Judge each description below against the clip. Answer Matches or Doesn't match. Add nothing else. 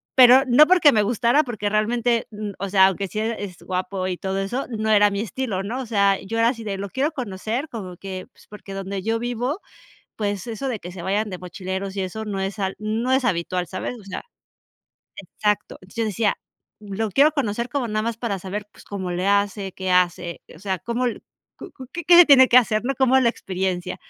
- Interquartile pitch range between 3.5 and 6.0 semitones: Matches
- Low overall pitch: Doesn't match